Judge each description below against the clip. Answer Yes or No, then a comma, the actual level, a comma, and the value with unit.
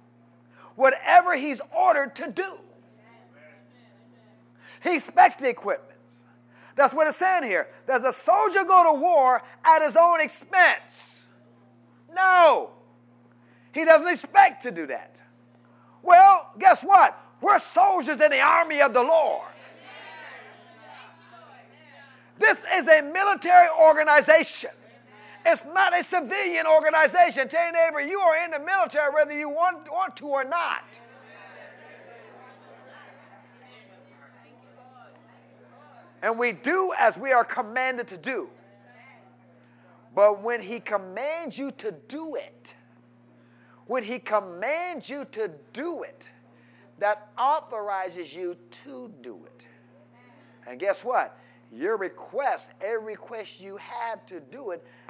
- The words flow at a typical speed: No, slow, 120 wpm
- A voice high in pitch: Yes, very high, 280 Hz